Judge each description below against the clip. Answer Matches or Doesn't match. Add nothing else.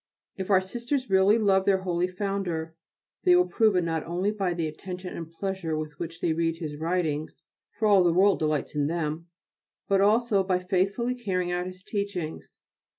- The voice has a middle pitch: Matches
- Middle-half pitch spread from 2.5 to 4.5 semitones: Matches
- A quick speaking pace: Doesn't match